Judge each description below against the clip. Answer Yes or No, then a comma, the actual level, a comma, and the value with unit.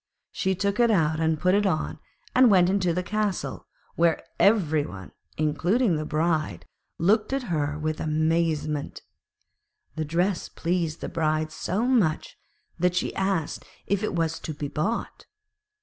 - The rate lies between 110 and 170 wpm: Yes, average, 150 wpm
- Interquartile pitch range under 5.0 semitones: Yes, average, 4.2 semitones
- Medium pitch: Yes, medium, 170 Hz